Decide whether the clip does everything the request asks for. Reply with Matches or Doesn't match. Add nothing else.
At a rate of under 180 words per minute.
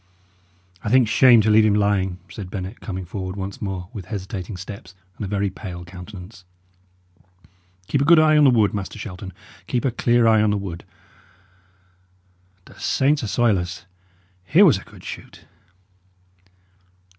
Matches